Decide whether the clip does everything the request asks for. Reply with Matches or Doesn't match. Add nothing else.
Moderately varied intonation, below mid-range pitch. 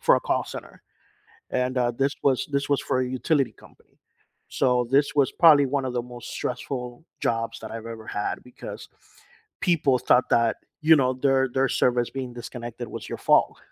Doesn't match